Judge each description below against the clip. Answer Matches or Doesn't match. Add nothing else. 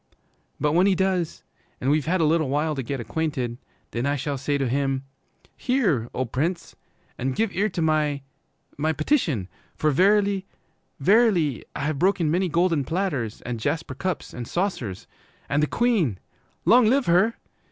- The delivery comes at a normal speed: Matches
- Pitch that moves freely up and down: Matches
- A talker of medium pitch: Matches